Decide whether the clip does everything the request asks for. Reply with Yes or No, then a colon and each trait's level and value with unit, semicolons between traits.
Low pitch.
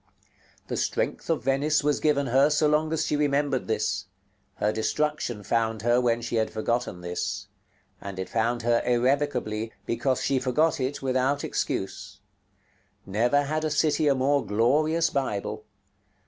Yes: low, 130 Hz